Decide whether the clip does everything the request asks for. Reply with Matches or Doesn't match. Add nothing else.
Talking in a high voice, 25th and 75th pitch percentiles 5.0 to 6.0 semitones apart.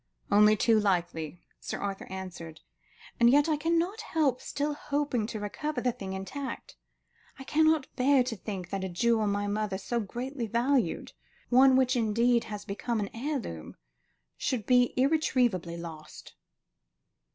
Matches